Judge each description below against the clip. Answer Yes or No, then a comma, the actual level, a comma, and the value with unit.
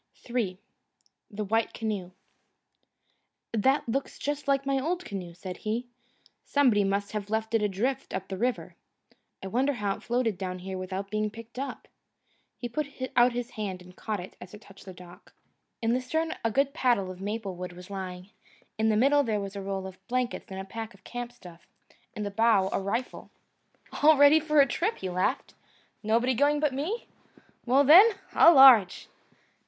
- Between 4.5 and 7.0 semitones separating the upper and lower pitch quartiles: Yes, average, 5.2 semitones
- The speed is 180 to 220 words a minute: Yes, average, 185 wpm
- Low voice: No, high, 220 Hz